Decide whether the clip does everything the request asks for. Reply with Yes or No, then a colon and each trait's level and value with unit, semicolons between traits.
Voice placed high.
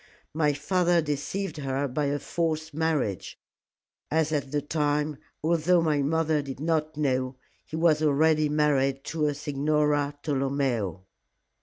No: medium, 150 Hz